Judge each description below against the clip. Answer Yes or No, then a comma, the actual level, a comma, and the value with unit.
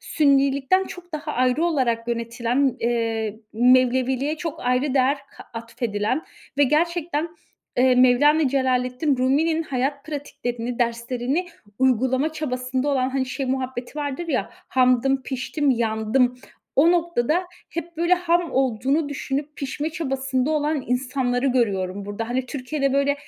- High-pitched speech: Yes, very high, 265 Hz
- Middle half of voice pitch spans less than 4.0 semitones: Yes, average, 3.2 semitones